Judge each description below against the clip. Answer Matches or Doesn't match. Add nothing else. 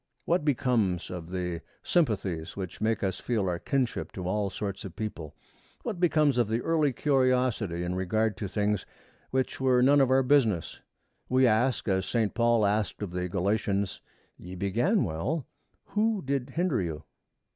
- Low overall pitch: Matches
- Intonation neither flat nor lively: Doesn't match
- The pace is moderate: Matches